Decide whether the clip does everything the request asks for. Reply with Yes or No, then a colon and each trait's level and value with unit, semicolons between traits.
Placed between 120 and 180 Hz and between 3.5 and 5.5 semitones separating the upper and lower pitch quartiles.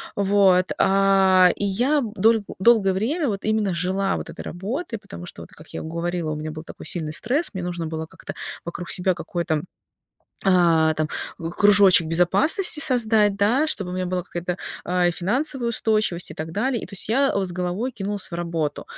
No: high, 190 Hz; average, 3.9 semitones